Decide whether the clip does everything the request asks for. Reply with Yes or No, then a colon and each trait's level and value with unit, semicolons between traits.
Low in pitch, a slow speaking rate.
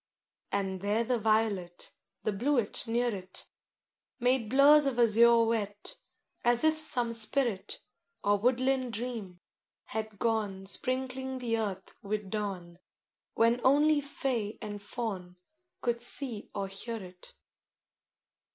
No: high, 225 Hz; slow, 125 wpm